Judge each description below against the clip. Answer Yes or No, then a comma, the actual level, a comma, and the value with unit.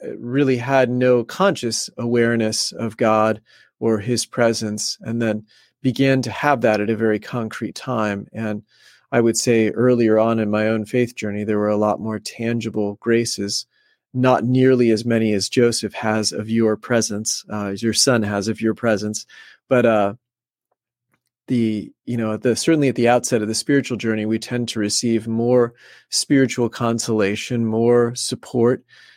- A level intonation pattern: Yes, narrow, 2.0 semitones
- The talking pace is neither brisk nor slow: Yes, average, 165 wpm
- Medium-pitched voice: No, low, 115 Hz